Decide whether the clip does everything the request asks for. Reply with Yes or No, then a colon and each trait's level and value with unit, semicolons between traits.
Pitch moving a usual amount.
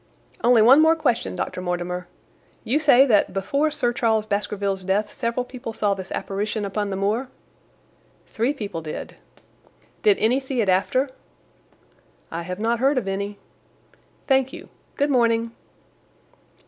Yes: average, 4.7 semitones